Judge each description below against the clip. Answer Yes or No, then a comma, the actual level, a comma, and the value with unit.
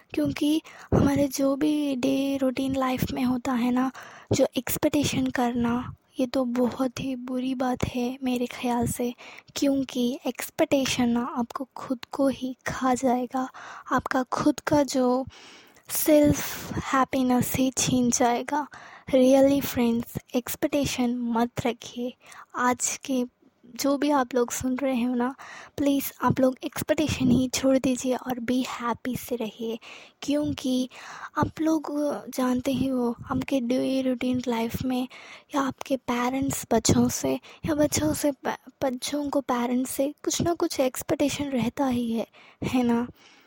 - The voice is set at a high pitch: Yes, very high, 260 Hz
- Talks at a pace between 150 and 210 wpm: No, average, 140 wpm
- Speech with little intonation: Yes, narrow, 1.9 semitones